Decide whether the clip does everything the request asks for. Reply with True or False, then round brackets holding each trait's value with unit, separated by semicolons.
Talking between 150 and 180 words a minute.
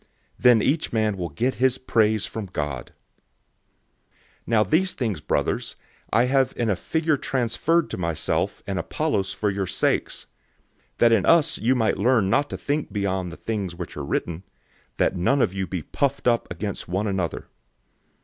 True (170 wpm)